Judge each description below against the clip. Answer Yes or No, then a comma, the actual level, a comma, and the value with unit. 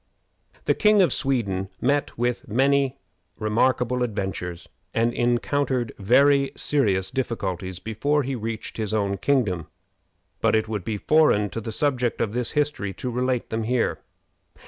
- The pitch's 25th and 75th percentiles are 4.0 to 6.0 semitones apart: Yes, average, 4.3 semitones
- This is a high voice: No, low, 120 Hz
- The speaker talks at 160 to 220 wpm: No, average, 145 wpm